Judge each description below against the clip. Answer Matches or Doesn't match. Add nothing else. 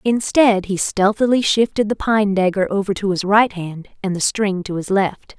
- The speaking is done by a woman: Matches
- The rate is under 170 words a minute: Doesn't match